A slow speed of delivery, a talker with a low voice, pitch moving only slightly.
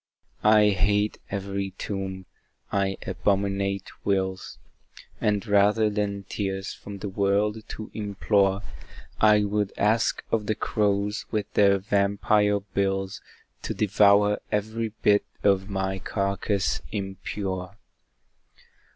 Yes: slow, 110 wpm; low, 100 Hz; narrow, 1.1 semitones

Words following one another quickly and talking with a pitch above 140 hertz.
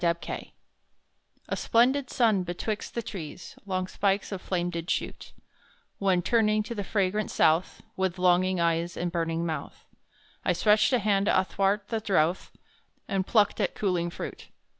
No: average, 150 wpm; high, 190 Hz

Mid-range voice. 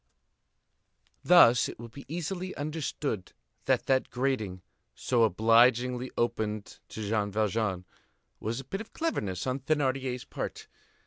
No: low, 125 Hz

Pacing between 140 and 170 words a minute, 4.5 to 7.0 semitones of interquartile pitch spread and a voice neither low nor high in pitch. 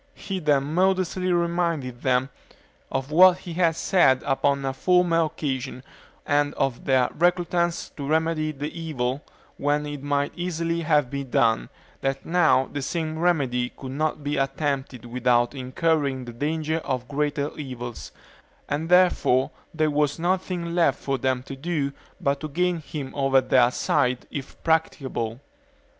No: average, 150 wpm; average, 3.9 semitones; medium, 145 Hz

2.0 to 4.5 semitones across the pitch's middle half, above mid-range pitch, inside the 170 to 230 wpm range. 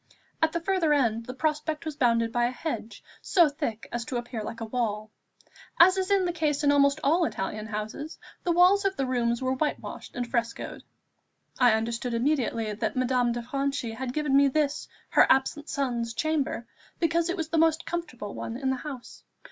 No: average, 4.9 semitones; very high, 265 Hz; average, 195 wpm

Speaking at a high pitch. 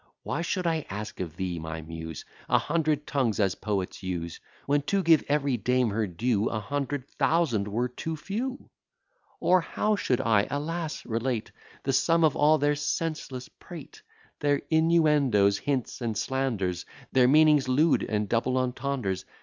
No: low, 130 Hz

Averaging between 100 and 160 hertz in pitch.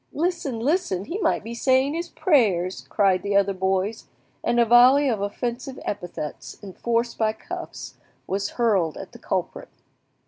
No: high, 230 Hz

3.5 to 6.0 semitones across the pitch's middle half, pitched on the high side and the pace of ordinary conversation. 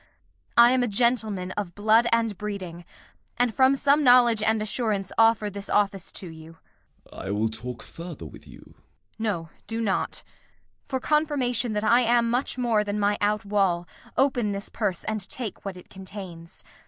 Yes: average, 3.8 semitones; high, 210 Hz; average, 175 wpm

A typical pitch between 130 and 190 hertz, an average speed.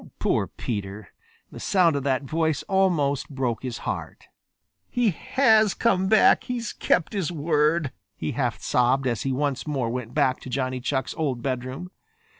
Yes: medium, 140 Hz; average, 160 wpm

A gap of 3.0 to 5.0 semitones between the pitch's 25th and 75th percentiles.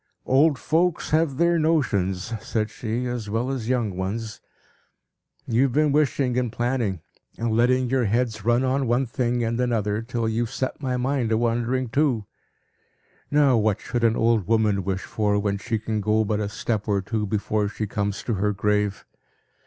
Yes: average, 3.3 semitones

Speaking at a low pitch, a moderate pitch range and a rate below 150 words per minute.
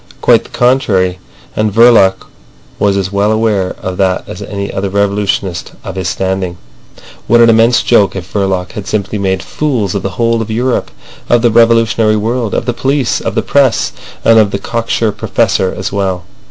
No: low, 105 Hz; average, 3.3 semitones; average, 180 wpm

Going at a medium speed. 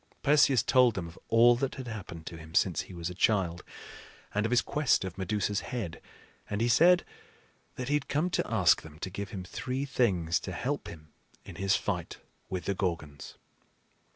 Yes: average, 195 wpm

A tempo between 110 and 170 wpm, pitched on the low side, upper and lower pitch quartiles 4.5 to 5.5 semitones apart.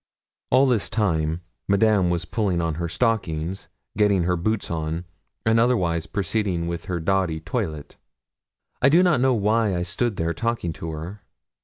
Yes: average, 160 wpm; very low, 95 Hz; average, 4.9 semitones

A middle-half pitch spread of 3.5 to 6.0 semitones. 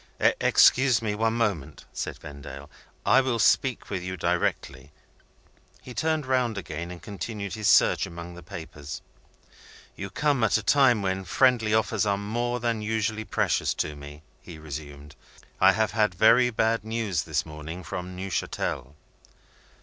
Yes: average, 5.1 semitones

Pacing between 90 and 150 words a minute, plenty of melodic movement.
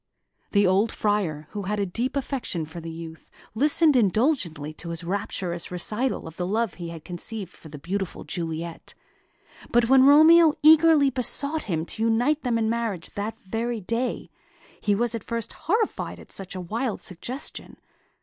No: average, 170 wpm; wide, 6.3 semitones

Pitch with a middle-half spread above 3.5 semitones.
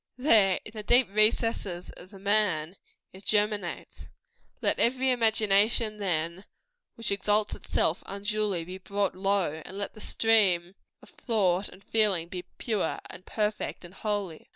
No: average, 2.7 semitones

